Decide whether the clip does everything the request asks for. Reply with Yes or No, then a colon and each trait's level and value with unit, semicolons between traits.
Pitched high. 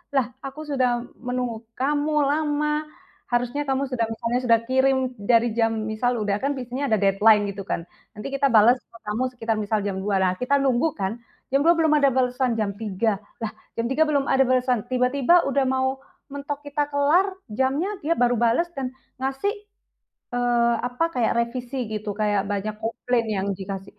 Yes: very high, 250 Hz